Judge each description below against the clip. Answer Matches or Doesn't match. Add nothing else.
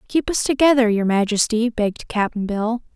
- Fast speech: Doesn't match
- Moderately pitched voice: Doesn't match